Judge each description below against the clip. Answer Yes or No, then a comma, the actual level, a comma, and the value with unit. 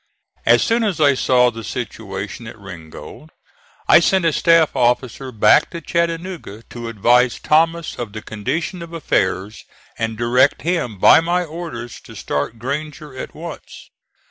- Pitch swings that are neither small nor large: No, wide, 6.7 semitones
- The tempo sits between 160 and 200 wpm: No, average, 150 wpm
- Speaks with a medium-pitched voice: No, low, 130 Hz